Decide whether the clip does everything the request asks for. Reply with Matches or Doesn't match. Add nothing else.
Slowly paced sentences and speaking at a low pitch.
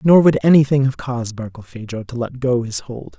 Doesn't match